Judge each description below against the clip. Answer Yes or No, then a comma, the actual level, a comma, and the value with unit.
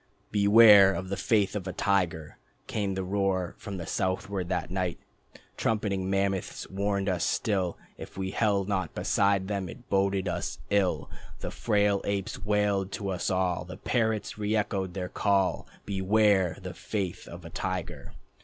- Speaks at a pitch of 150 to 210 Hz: No, low, 100 Hz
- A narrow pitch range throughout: Yes, narrow, 1.6 semitones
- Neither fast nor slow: Yes, average, 160 wpm